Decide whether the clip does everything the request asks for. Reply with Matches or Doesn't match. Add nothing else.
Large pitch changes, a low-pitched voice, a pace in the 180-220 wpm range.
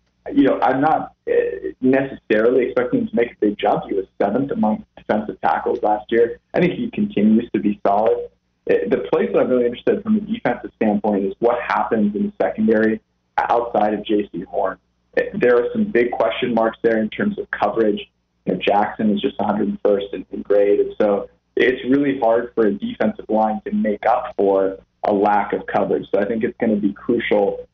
Matches